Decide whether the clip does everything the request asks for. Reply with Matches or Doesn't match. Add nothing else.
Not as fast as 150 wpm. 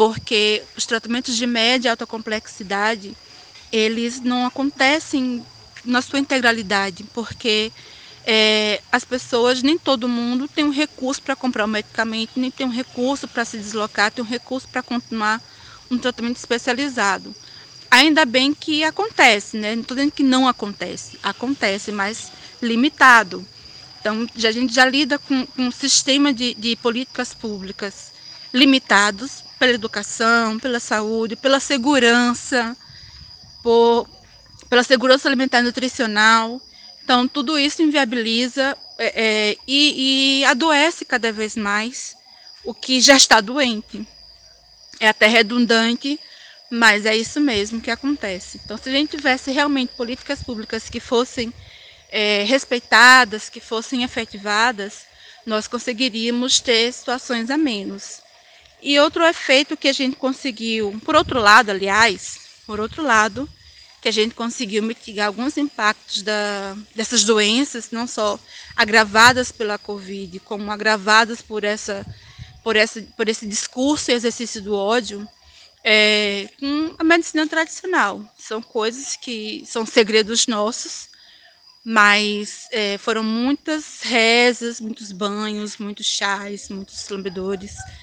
Matches